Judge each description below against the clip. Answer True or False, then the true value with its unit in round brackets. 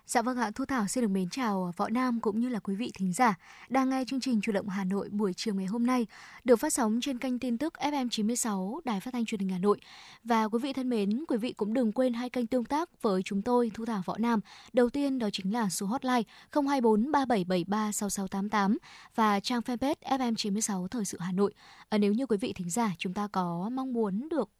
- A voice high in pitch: True (230 Hz)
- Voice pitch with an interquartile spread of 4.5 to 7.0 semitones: False (3.8 semitones)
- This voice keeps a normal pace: True (230 wpm)